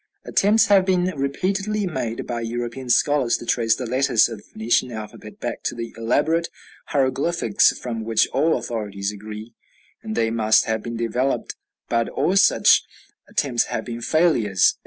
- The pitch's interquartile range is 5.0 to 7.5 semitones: Yes, wide, 5.6 semitones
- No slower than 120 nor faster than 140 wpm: No, average, 155 wpm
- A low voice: Yes, low, 120 Hz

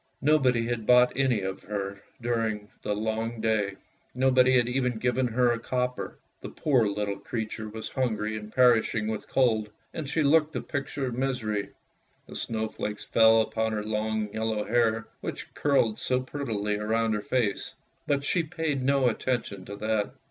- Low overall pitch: Yes, low, 115 Hz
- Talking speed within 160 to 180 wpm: Yes, average, 170 wpm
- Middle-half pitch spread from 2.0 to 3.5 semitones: Yes, average, 3.1 semitones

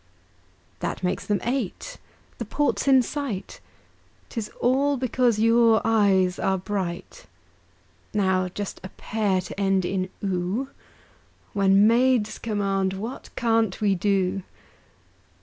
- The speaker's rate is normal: No, slow, 115 wpm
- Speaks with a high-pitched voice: Yes, high, 205 Hz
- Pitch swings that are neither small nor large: Yes, average, 3.5 semitones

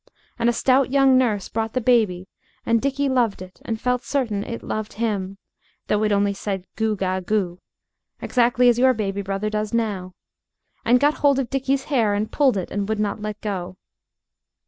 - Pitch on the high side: Yes, high, 220 Hz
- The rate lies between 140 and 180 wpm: No, average, 190 wpm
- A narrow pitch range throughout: No, average, 3.8 semitones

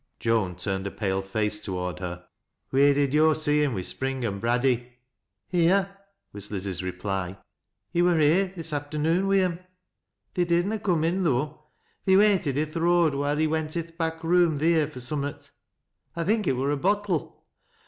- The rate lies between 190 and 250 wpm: Yes, average, 200 wpm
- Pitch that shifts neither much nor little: No, wide, 7.2 semitones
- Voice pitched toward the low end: No, medium, 150 Hz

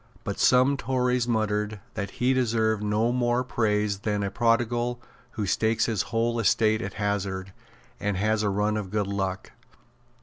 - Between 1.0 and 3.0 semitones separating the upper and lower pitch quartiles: Yes, narrow, 2.6 semitones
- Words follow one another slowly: No, average, 160 wpm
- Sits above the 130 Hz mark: No, low, 110 Hz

